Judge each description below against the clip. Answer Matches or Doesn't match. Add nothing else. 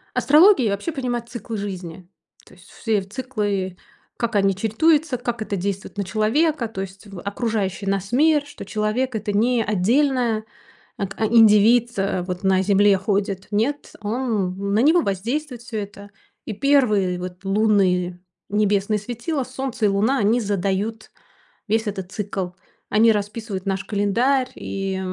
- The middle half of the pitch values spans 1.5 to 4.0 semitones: Matches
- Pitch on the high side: Matches